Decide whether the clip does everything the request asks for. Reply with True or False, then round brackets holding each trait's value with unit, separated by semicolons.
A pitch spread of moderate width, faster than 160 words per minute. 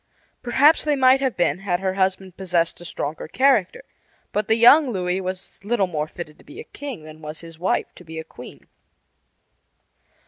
False (6.4 semitones; 185 wpm)